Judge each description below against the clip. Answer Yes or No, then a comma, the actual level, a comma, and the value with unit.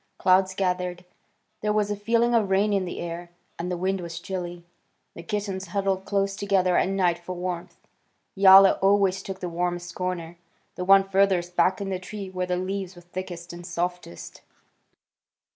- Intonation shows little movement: Yes, narrow, 1.8 semitones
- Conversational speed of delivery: Yes, average, 175 wpm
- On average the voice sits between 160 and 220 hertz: Yes, medium, 185 Hz